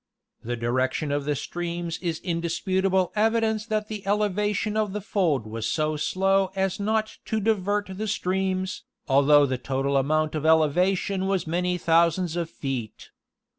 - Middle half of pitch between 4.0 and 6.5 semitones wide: Yes, average, 4.6 semitones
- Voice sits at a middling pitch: Yes, medium, 180 Hz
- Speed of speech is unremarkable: Yes, average, 150 wpm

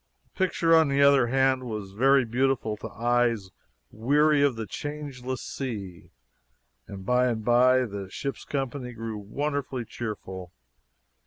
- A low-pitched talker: Yes, low, 125 Hz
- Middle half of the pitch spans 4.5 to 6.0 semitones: No, average, 3.9 semitones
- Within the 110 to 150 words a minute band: Yes, average, 140 wpm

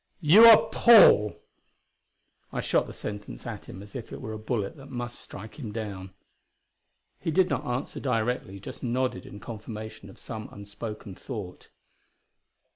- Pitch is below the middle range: Yes, low, 110 Hz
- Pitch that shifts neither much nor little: Yes, average, 3.9 semitones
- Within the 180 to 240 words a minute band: No, average, 155 wpm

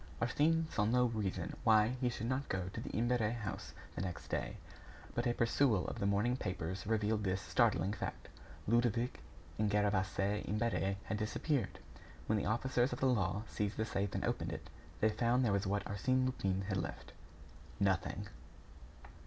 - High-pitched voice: No, low, 105 Hz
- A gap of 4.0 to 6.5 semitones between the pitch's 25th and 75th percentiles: No, average, 3.4 semitones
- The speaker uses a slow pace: No, average, 170 wpm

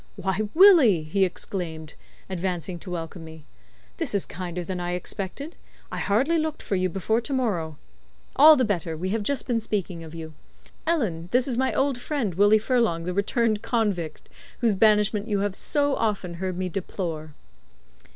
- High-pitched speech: Yes, high, 195 Hz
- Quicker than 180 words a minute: No, average, 170 wpm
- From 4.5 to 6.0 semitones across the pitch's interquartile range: Yes, average, 5.2 semitones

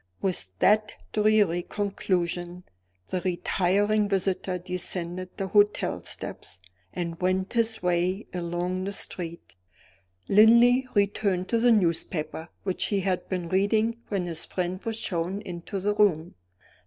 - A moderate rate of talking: No, slow, 130 wpm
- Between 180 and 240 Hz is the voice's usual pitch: Yes, medium, 185 Hz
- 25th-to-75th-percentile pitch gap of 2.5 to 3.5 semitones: Yes, average, 2.8 semitones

